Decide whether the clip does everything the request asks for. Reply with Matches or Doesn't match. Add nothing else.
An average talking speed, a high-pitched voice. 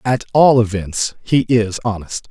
Doesn't match